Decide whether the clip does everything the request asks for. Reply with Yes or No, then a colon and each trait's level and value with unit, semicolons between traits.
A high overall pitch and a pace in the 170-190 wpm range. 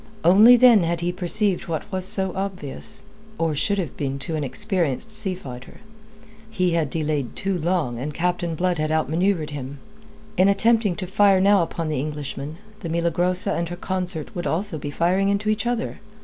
No: medium, 175 Hz; average, 180 wpm